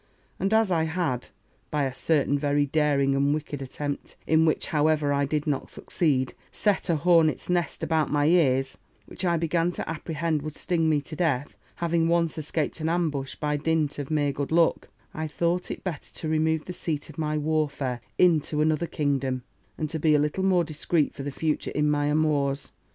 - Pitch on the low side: No, medium, 155 Hz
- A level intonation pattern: Yes, narrow, 2.3 semitones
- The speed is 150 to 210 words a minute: Yes, average, 195 wpm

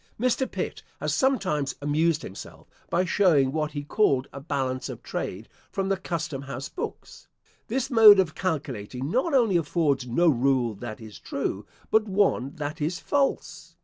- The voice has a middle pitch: Yes, medium, 155 Hz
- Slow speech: No, average, 160 wpm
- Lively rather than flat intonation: Yes, wide, 6.2 semitones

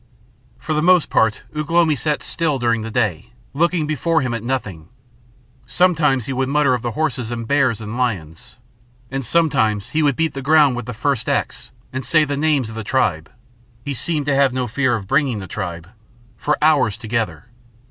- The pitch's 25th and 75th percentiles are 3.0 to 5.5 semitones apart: Yes, average, 5.1 semitones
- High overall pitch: No, low, 130 Hz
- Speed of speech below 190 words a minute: No, average, 195 wpm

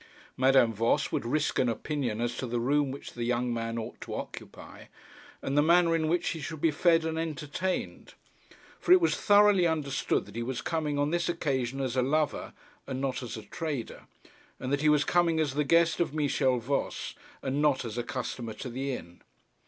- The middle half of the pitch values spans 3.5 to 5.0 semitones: Yes, average, 4.5 semitones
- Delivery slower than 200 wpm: No, fast, 205 wpm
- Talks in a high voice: No, medium, 140 Hz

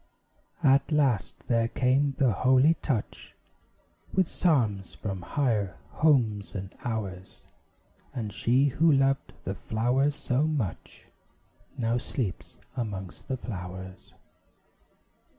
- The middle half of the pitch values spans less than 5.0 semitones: No, wide, 5.4 semitones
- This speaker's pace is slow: Yes, slow, 105 wpm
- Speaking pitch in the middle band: No, low, 120 Hz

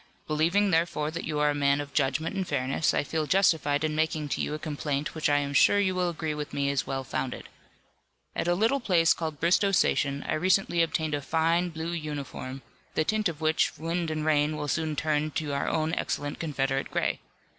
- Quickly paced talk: Yes, fast, 210 wpm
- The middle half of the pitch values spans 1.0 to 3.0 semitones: Yes, narrow, 2.5 semitones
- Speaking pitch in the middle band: Yes, medium, 155 Hz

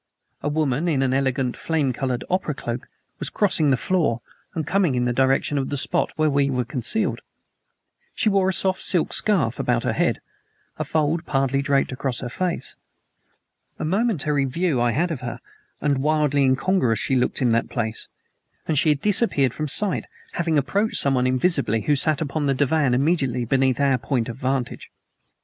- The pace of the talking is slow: No, average, 180 wpm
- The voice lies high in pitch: No, medium, 140 Hz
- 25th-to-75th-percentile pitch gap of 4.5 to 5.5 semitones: No, average, 3.9 semitones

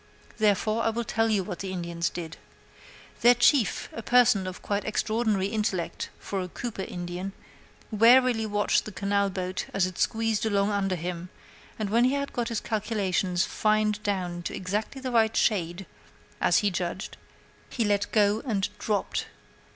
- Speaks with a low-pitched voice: No, high, 205 Hz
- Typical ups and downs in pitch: Yes, average, 3.2 semitones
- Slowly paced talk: No, average, 165 wpm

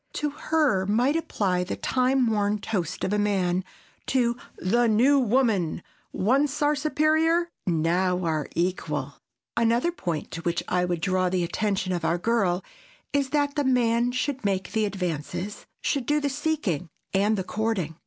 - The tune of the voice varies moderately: No, wide, 6.7 semitones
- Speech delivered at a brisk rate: No, average, 155 wpm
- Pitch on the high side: Yes, high, 210 Hz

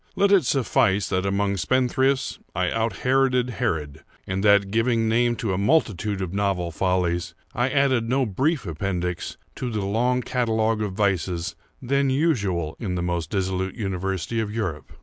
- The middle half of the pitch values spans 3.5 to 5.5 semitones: Yes, average, 5.1 semitones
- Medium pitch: No, low, 105 Hz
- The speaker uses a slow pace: No, average, 160 wpm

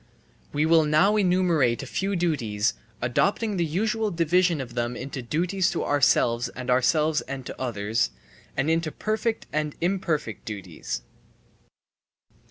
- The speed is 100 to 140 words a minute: Yes, slow, 135 wpm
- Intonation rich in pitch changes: Yes, wide, 6.6 semitones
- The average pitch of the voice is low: No, medium, 155 Hz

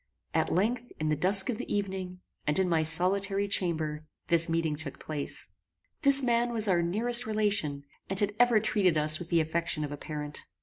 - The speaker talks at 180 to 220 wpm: Yes, average, 190 wpm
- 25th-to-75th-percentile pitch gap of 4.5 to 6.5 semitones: Yes, average, 5.0 semitones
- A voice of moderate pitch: Yes, medium, 180 Hz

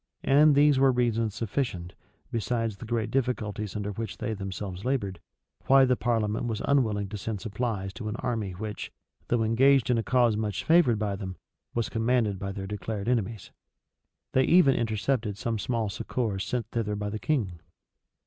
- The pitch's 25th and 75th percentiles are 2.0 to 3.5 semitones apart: Yes, average, 3.2 semitones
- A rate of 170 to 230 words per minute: Yes, average, 175 wpm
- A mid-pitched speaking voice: No, low, 110 Hz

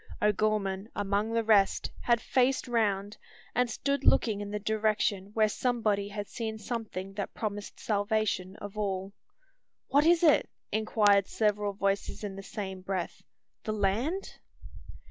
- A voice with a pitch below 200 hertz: No, high, 210 Hz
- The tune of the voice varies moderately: No, narrow, 2.1 semitones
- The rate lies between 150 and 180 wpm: No, average, 140 wpm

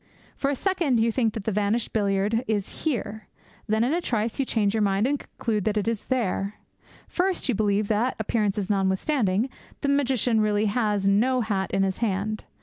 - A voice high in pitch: Yes, high, 215 Hz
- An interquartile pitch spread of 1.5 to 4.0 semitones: Yes, average, 3.4 semitones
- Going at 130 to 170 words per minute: No, average, 195 wpm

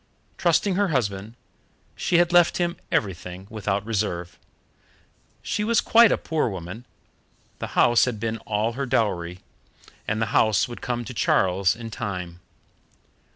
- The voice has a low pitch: Yes, low, 110 Hz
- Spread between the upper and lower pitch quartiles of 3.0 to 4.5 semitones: No, average, 5.1 semitones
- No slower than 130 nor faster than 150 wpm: Yes, average, 145 wpm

